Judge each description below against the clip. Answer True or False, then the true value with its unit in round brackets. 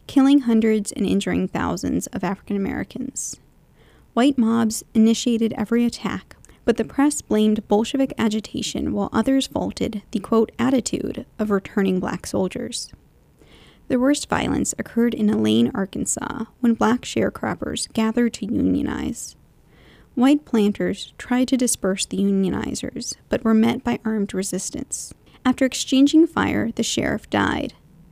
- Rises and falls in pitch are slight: False (3.7 semitones)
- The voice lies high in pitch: True (225 Hz)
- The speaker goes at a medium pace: False (130 wpm)